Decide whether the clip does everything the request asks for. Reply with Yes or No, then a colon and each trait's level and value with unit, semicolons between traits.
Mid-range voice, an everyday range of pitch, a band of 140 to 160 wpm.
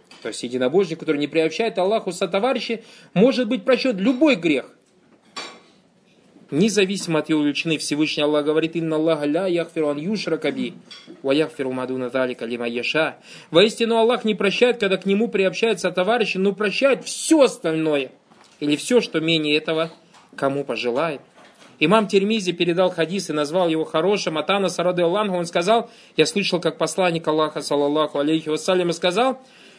No: medium, 175 Hz; wide, 5.7 semitones; average, 145 wpm